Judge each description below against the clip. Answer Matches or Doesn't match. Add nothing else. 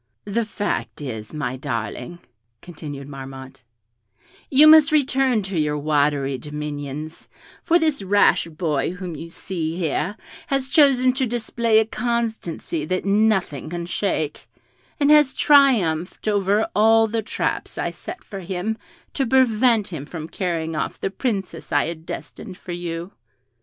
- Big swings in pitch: Matches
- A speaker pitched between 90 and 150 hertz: Doesn't match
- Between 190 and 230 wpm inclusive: Doesn't match